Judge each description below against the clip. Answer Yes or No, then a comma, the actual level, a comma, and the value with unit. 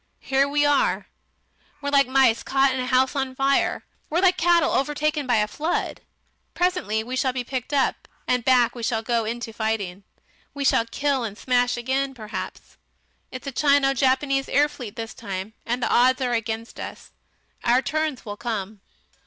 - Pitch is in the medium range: No, very high, 255 Hz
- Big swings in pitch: No, average, 3.3 semitones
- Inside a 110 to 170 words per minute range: No, average, 180 wpm